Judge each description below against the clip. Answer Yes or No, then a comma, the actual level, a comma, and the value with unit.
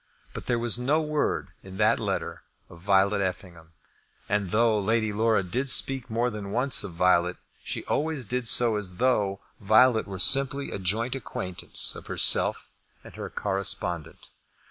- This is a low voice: Yes, low, 105 Hz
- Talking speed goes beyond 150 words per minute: Yes, average, 160 wpm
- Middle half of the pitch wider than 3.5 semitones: Yes, average, 4.3 semitones